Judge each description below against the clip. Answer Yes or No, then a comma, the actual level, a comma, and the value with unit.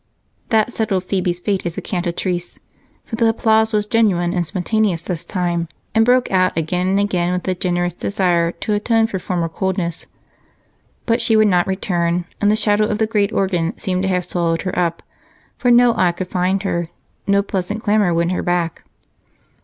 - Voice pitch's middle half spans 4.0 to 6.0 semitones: No, average, 3.2 semitones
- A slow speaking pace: No, average, 185 wpm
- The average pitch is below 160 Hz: No, medium, 185 Hz